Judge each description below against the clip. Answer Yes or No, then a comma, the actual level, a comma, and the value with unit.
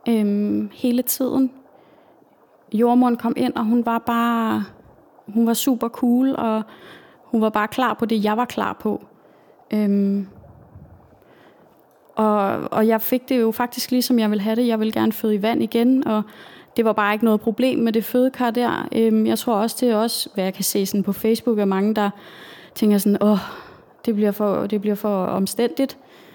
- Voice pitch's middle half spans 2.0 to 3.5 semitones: Yes, narrow, 2.6 semitones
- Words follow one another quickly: No, average, 190 wpm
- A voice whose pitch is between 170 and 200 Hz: No, high, 225 Hz